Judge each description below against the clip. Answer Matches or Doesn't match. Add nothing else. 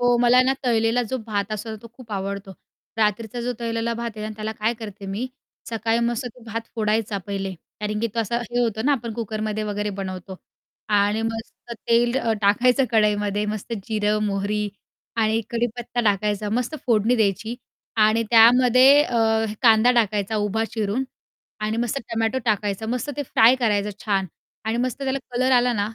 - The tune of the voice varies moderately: Doesn't match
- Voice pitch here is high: Matches